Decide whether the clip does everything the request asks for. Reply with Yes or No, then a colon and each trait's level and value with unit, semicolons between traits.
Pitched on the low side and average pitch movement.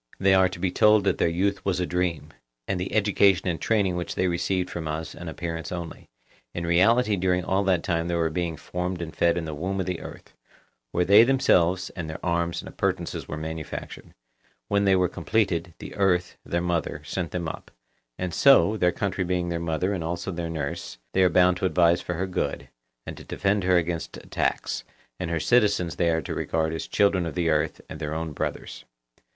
No: very low, 90 Hz; narrow, 2.2 semitones